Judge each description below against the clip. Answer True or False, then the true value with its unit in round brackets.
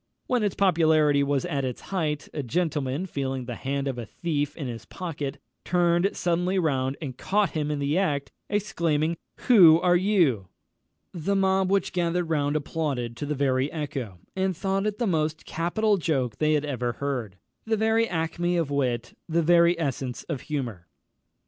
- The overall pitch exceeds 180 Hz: False (155 Hz)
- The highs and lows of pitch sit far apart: False (4.4 semitones)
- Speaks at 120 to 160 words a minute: False (175 wpm)